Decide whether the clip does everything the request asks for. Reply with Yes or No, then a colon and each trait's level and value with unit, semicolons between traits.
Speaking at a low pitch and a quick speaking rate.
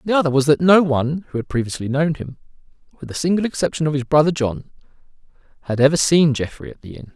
No: medium, 150 Hz; fast, 220 wpm